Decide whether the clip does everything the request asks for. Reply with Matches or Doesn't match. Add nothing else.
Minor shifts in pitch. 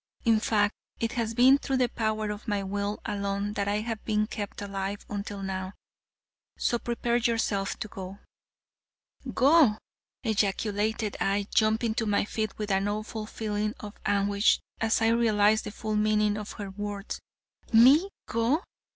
Matches